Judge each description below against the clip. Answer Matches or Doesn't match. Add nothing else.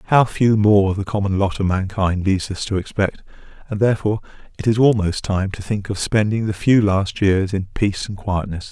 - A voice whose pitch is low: Matches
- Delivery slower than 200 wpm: Doesn't match